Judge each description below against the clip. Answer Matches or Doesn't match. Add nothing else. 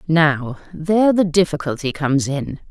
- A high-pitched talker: Doesn't match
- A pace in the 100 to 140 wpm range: Matches